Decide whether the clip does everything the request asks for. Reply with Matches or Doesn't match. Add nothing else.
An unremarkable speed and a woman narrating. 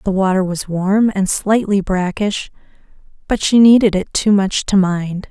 Matches